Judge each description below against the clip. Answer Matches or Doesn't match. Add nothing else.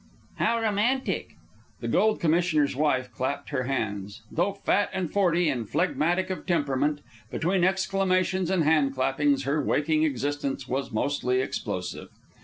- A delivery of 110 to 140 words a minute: Matches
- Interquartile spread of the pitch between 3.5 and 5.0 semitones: Doesn't match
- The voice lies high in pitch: Doesn't match